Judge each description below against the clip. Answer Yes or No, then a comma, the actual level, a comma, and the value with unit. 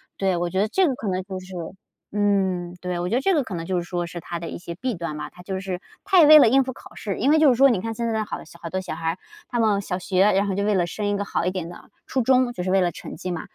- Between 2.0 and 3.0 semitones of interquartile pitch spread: No, average, 4.2 semitones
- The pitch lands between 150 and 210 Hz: Yes, high, 195 Hz